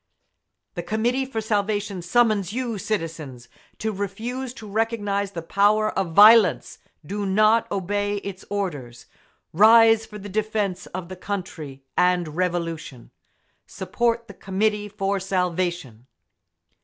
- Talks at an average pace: No, slow, 120 wpm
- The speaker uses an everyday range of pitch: Yes, average, 3.4 semitones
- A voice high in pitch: Yes, high, 200 Hz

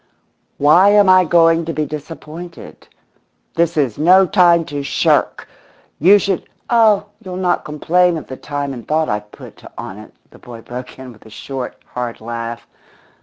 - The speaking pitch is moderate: Yes, medium, 155 Hz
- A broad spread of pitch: Yes, wide, 5.8 semitones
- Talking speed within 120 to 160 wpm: No, average, 170 wpm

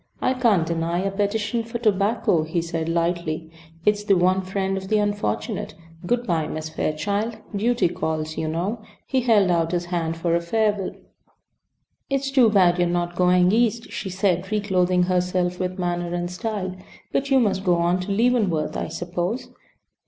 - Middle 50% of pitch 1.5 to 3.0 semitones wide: No, average, 3.4 semitones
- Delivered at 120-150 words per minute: No, average, 175 wpm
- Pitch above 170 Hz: Yes, medium, 185 Hz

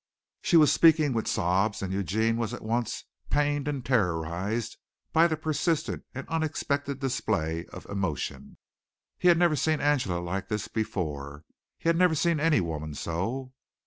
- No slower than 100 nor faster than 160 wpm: Yes, average, 155 wpm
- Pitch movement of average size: No, wide, 8.1 semitones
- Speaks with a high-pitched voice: No, low, 120 Hz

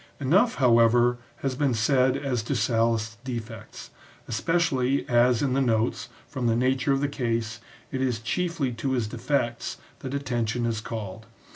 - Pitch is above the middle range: No, low, 125 Hz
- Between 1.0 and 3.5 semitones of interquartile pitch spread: Yes, average, 2.9 semitones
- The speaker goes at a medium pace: Yes, average, 160 wpm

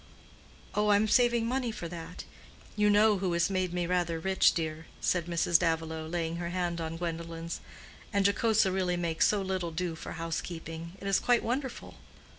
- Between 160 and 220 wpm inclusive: Yes, average, 175 wpm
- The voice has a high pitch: No, medium, 175 Hz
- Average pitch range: Yes, average, 3.4 semitones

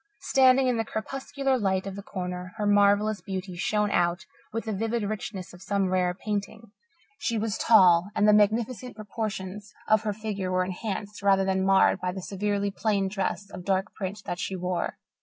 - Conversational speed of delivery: Yes, average, 185 wpm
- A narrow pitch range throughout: Yes, narrow, 2.3 semitones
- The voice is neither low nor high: No, high, 200 Hz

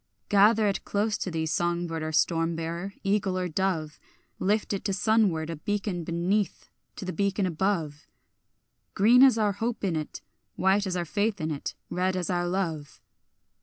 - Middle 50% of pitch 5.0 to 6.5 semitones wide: No, average, 3.6 semitones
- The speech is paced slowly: No, average, 175 wpm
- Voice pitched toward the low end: No, medium, 185 Hz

